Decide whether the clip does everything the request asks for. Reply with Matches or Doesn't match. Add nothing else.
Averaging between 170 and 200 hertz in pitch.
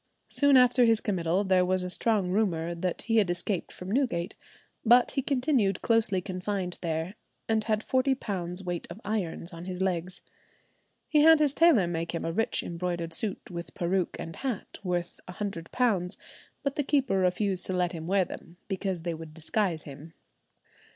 Matches